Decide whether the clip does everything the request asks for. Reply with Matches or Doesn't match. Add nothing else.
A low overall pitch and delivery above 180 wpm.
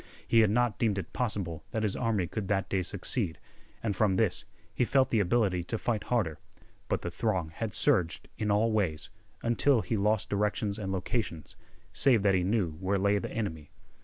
Matches